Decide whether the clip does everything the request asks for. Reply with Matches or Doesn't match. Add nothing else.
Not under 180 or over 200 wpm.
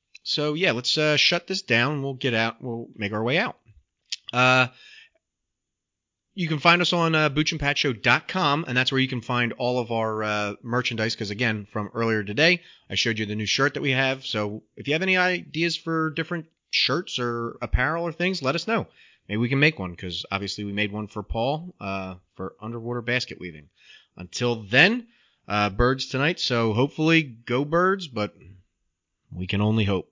Matches